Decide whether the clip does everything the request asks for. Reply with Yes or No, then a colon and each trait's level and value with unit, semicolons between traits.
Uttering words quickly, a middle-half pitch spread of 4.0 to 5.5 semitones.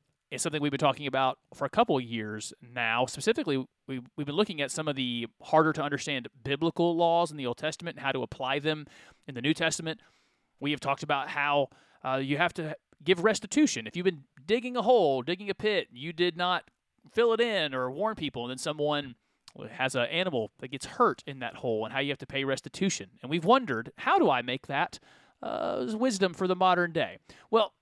Yes: fast, 220 wpm; average, 4.9 semitones